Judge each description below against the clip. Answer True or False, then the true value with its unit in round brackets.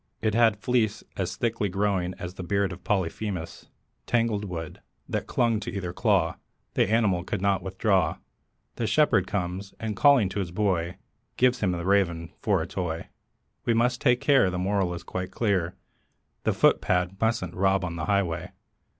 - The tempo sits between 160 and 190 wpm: True (170 wpm)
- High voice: False (95 Hz)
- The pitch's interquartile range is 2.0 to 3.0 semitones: False (3.4 semitones)